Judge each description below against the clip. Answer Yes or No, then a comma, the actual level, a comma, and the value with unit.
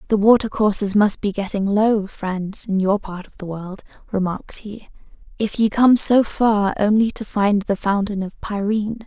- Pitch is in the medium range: No, high, 205 Hz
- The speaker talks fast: No, average, 180 wpm